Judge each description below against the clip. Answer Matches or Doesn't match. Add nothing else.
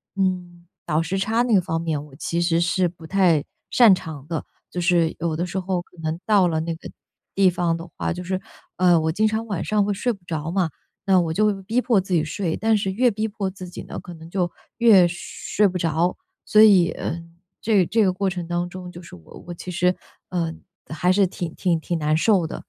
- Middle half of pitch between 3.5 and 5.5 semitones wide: Doesn't match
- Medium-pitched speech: Matches